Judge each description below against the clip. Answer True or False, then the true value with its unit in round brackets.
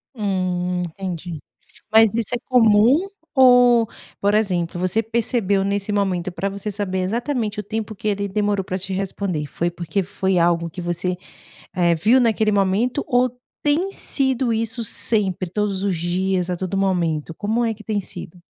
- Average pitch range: True (3.5 semitones)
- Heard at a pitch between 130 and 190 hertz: False (200 Hz)